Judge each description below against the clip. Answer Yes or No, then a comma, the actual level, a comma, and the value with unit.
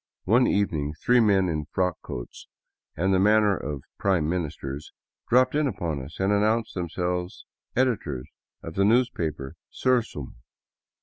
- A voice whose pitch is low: Yes, very low, 95 Hz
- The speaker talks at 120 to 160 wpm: Yes, average, 140 wpm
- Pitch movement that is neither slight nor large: No, wide, 5.9 semitones